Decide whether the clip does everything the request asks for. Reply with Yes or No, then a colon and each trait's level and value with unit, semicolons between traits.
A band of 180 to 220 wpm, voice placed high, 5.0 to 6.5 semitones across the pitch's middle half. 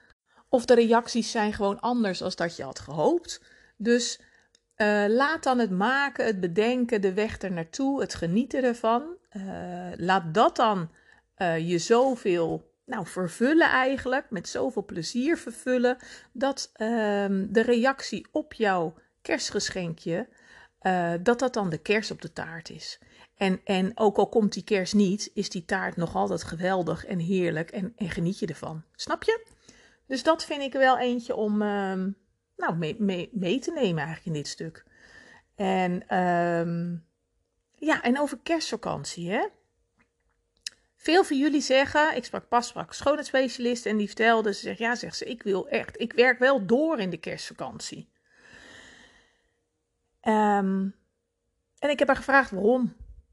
No: average, 155 wpm; high, 215 Hz; average, 5.3 semitones